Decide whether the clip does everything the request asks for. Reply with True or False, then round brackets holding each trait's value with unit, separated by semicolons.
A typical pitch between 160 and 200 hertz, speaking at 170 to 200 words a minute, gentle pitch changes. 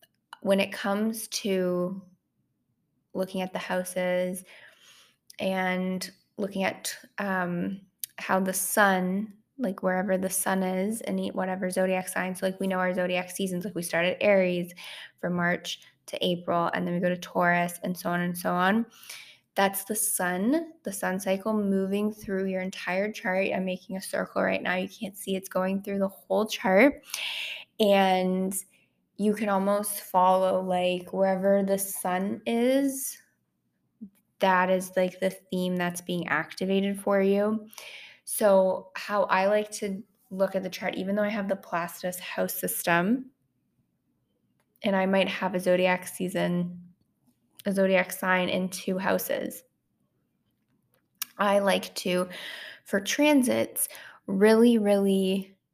False (190 Hz; 145 wpm; 1.7 semitones)